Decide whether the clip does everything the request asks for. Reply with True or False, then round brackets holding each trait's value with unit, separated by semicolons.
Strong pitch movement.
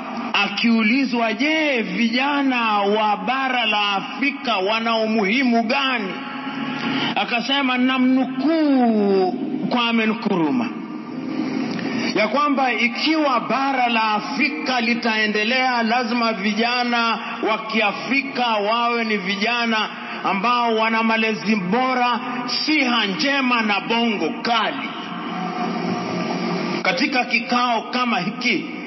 False (3.1 semitones)